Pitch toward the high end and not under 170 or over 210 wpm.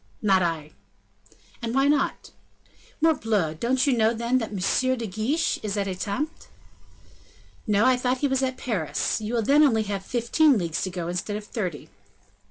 Yes: high, 225 Hz; average, 175 wpm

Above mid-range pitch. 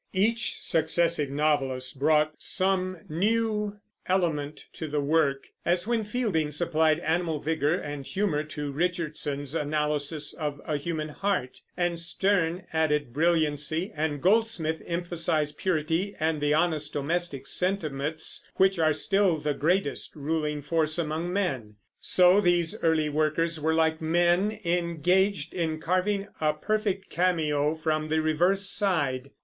No: medium, 160 Hz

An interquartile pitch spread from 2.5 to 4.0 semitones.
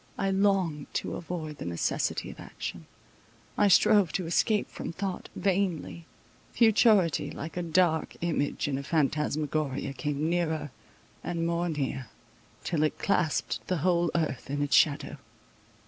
Yes: average, 3.4 semitones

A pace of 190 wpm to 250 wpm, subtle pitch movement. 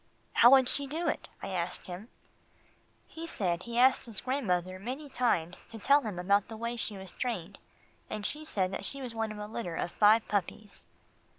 No: fast, 205 wpm; average, 5.1 semitones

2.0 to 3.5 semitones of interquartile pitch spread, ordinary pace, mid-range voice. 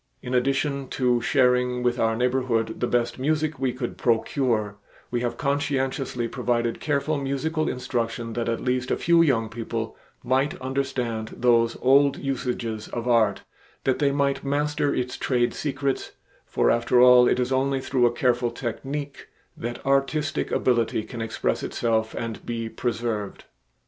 No: average, 2.7 semitones; average, 150 wpm; low, 125 Hz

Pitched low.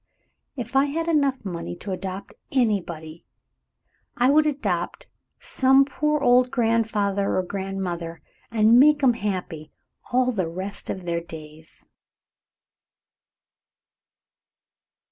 No: high, 210 Hz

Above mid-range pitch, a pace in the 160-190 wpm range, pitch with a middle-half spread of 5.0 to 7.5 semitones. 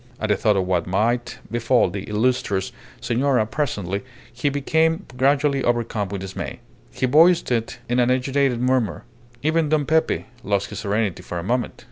No: low, 120 Hz; average, 165 wpm; average, 5.3 semitones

